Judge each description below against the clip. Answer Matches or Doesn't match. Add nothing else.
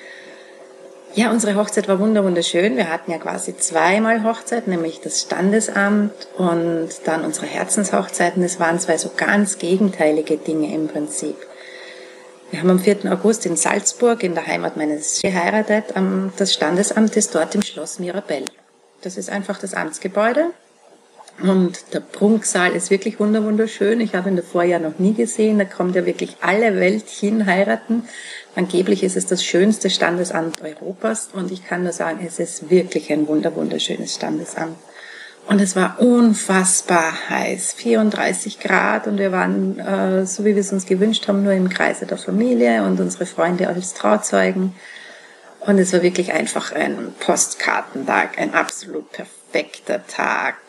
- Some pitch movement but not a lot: Matches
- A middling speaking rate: Matches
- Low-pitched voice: Doesn't match